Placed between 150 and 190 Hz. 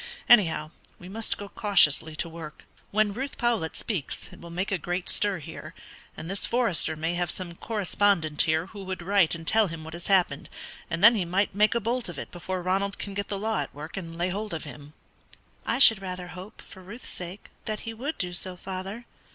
Yes: medium, 185 Hz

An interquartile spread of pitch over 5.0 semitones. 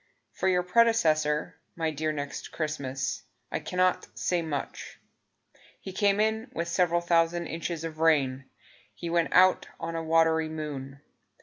No: narrow, 2.5 semitones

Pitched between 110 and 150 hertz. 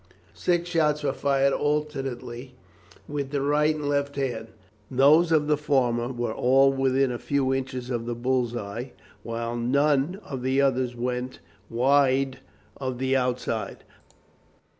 Yes: low, 135 Hz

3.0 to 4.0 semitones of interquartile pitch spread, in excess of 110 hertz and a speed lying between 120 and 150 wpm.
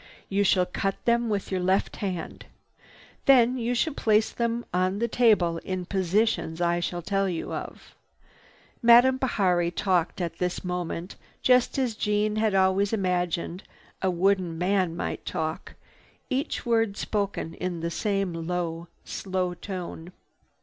Yes: average, 3.5 semitones; high, 190 Hz; average, 145 wpm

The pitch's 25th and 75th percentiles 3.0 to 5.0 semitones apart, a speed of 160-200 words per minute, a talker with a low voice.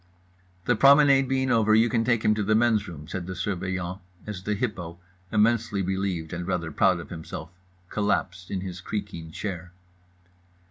Yes: average, 3.6 semitones; average, 170 wpm; very low, 95 Hz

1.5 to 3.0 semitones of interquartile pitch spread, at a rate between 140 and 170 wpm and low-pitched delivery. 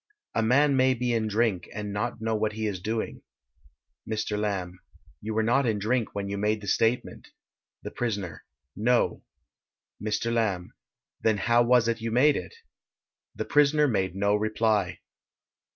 Yes: narrow, 2.6 semitones; average, 160 wpm; low, 110 Hz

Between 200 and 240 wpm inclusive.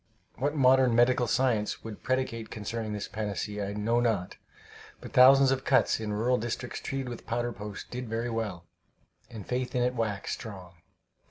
No: average, 170 wpm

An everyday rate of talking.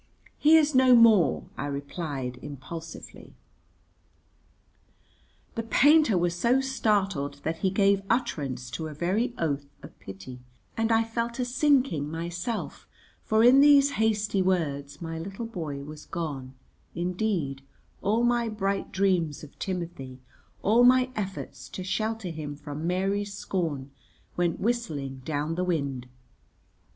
No: slow, 130 wpm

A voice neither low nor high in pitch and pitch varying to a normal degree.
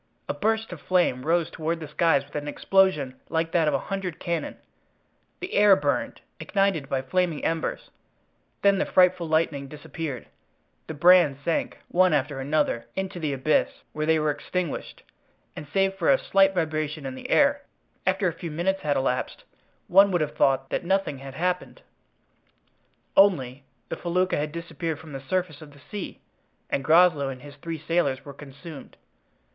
Yes: medium, 160 Hz; average, 4.1 semitones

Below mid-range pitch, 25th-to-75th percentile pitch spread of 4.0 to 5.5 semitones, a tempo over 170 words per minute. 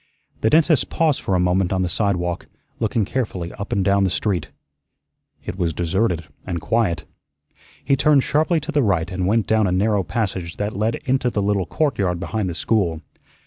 Yes: low, 100 Hz; average, 4.3 semitones; average, 190 wpm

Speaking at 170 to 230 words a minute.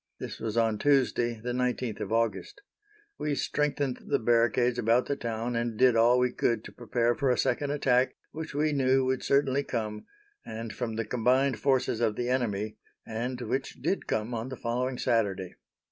Yes: average, 180 wpm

